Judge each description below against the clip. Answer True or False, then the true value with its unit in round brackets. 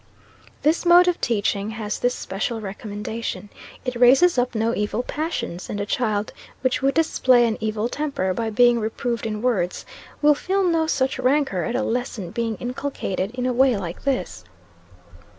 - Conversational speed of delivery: True (170 wpm)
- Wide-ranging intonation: False (4.0 semitones)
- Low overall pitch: False (240 Hz)